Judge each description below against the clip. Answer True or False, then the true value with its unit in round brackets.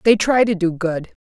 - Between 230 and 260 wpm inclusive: True (245 wpm)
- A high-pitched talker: True (195 Hz)